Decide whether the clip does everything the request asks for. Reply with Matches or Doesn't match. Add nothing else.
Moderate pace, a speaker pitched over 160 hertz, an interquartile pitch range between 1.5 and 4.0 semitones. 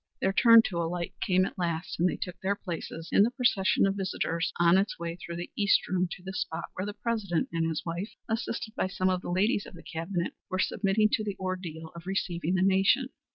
Doesn't match